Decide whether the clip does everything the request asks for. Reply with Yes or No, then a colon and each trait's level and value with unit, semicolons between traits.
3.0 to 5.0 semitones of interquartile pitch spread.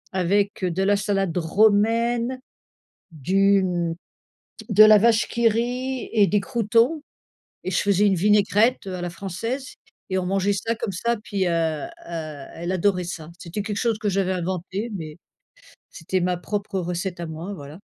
Yes: average, 3.3 semitones